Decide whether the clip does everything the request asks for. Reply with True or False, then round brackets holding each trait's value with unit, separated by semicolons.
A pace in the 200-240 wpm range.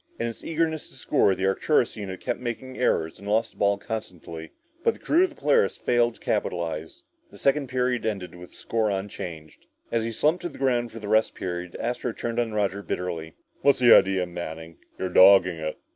True (205 wpm)